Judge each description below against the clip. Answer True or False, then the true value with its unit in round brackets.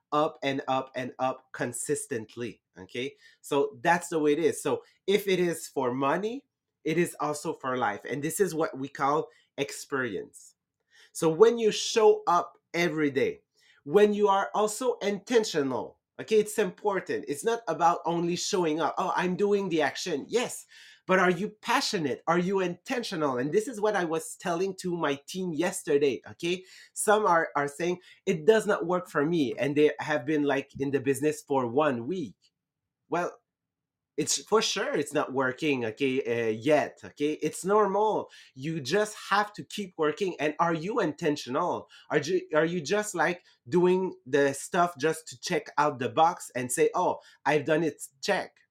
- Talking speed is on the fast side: False (175 wpm)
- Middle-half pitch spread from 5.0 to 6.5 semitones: True (5.6 semitones)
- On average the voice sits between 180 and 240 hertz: False (165 Hz)